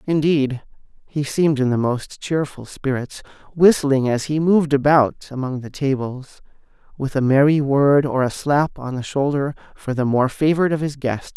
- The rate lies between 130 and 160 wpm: No, average, 175 wpm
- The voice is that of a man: Yes, male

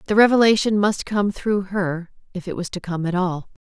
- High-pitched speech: Yes, high, 195 Hz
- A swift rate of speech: Yes, fast, 210 wpm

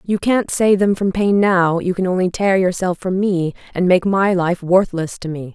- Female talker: Yes, female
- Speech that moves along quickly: Yes, fast, 225 wpm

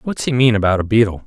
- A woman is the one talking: No, male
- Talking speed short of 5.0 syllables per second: No, 6.8 syllables/s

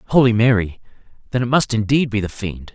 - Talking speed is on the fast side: No, average, 195 wpm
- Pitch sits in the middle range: No, low, 115 Hz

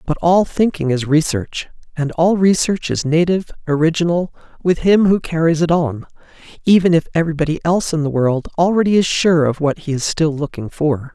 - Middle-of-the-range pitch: Yes, medium, 165 Hz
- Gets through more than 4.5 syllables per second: Yes, 5.5 syllables/s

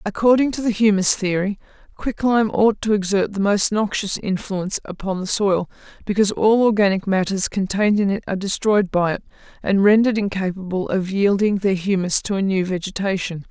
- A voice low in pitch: No, high, 200 Hz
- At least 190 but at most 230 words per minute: No, average, 175 wpm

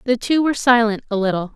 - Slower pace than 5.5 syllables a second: No, 6.8 syllables/s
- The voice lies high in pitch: Yes, high, 230 Hz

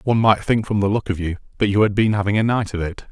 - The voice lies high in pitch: No, low, 105 Hz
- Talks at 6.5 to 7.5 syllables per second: Yes, 6.8 syllables/s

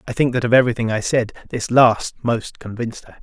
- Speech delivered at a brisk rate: Yes, fast, 225 wpm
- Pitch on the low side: Yes, low, 115 Hz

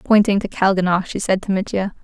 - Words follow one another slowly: No, fast, 205 wpm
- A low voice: No, high, 195 Hz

